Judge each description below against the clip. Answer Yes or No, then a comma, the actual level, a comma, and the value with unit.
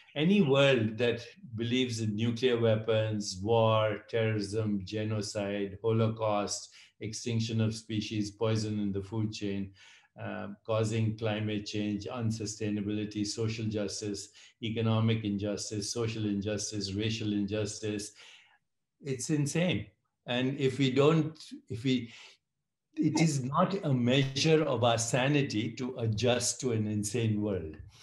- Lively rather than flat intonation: No, average, 2.7 semitones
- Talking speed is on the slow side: Yes, slow, 115 wpm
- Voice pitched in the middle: No, low, 110 Hz